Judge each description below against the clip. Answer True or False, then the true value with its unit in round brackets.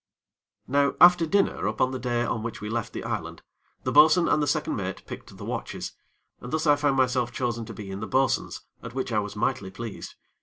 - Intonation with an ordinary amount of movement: True (4.2 semitones)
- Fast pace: True (220 wpm)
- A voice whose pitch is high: False (125 Hz)